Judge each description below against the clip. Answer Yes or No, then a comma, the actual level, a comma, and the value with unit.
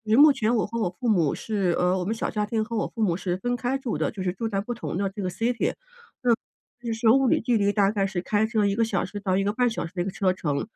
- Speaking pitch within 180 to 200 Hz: No, high, 210 Hz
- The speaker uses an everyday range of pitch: Yes, average, 3.4 semitones